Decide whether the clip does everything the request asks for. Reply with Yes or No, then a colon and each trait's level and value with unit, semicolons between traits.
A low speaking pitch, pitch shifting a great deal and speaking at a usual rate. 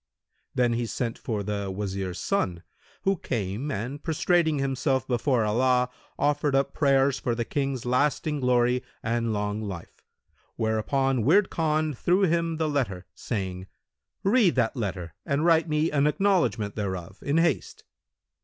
Yes: low, 130 Hz; wide, 6.0 semitones; average, 145 wpm